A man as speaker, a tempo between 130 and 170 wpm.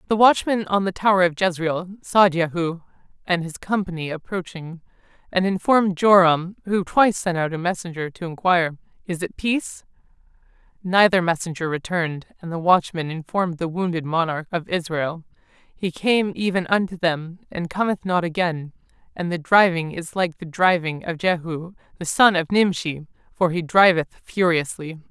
No: female; average, 155 wpm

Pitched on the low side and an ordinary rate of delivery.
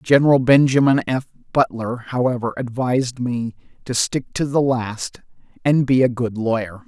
Yes: low, 125 Hz; average, 150 wpm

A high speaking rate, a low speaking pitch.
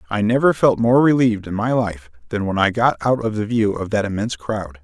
Yes: fast, 250 wpm; low, 110 Hz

